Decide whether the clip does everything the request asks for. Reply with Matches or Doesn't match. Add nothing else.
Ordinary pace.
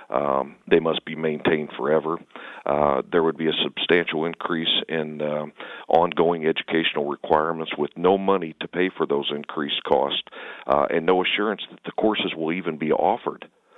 Matches